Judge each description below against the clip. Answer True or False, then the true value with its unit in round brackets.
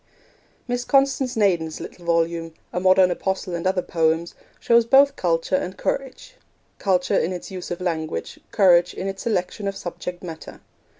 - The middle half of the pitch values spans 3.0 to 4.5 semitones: True (3.3 semitones)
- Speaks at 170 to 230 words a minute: False (160 wpm)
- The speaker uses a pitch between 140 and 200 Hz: True (185 Hz)